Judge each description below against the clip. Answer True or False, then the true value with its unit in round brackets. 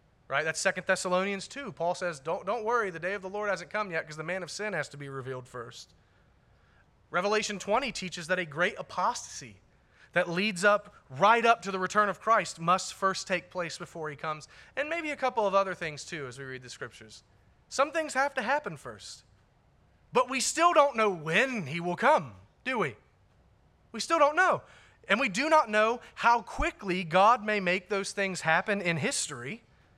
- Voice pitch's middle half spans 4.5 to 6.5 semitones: True (5.3 semitones)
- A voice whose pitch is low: False (190 Hz)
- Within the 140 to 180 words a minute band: False (200 wpm)